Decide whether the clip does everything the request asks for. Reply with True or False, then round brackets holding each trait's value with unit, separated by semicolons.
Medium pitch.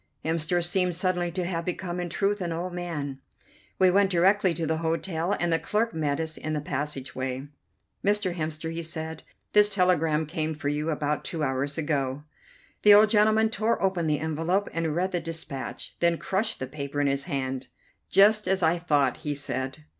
True (165 Hz)